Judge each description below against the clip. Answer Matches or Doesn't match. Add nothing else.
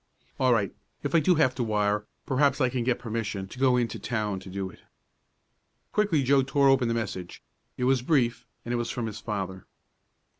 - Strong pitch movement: Doesn't match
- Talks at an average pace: Doesn't match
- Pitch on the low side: Matches